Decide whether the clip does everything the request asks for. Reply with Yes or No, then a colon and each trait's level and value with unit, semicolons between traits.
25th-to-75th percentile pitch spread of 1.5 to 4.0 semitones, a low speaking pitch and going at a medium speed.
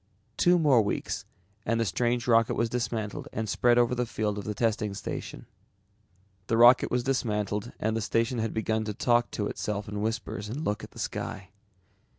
Yes: narrow, 2.4 semitones; low, 115 Hz; average, 185 wpm